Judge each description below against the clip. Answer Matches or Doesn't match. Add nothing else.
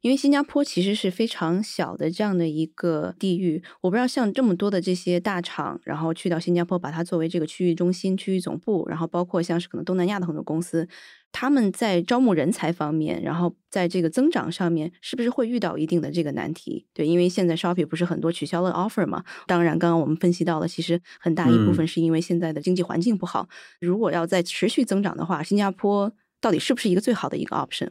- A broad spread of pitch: Doesn't match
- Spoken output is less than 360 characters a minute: Doesn't match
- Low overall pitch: Doesn't match